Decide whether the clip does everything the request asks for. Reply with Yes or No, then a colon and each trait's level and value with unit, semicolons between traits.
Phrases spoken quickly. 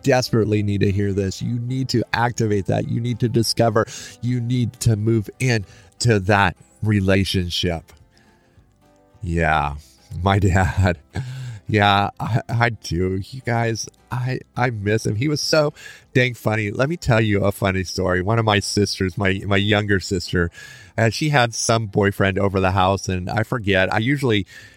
No: average, 165 wpm